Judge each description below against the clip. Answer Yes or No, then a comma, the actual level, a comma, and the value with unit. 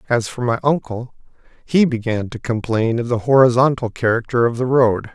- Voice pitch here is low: Yes, low, 120 Hz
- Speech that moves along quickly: No, average, 175 wpm